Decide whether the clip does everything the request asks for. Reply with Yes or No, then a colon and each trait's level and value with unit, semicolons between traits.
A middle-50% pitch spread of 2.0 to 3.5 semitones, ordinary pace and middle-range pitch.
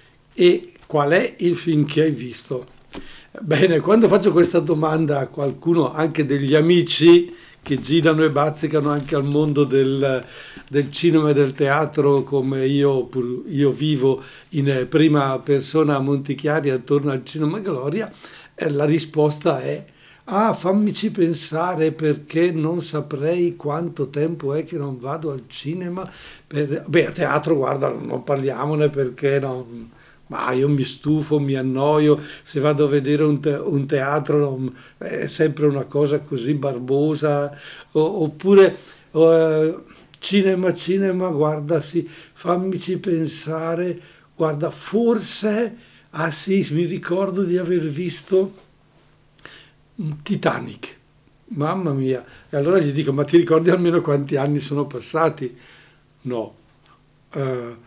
Yes: average, 3.1 semitones; average, 125 wpm; medium, 150 Hz